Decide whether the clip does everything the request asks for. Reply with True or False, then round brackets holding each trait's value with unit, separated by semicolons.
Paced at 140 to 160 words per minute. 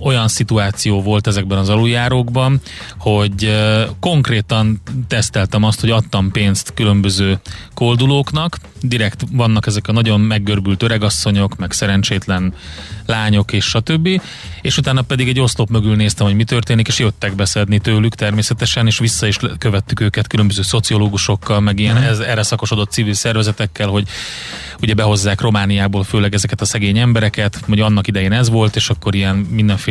True (150 wpm)